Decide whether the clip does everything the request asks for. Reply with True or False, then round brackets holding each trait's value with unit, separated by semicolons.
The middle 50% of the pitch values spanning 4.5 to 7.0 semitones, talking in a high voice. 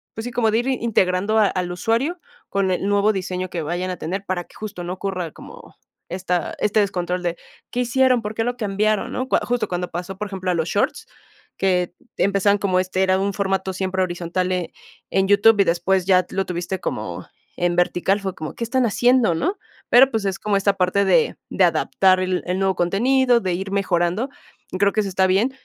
False (2.9 semitones; 195 Hz)